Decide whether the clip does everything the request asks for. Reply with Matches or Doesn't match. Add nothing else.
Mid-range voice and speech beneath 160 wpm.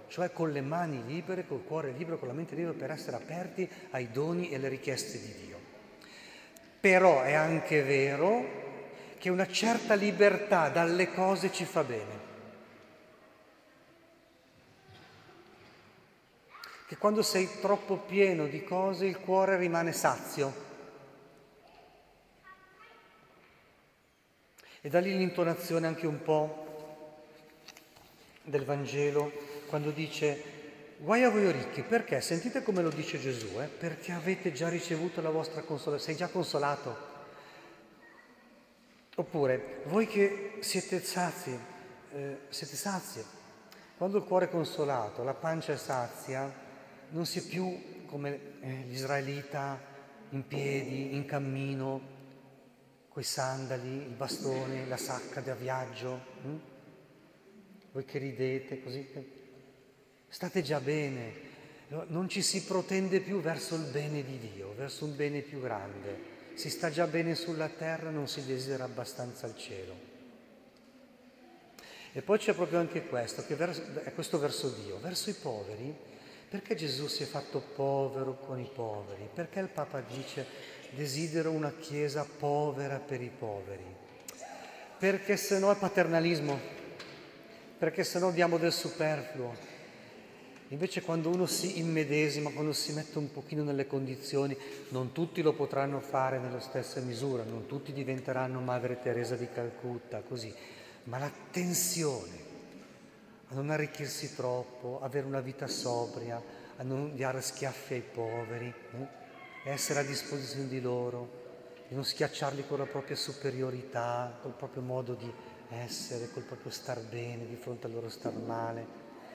Matches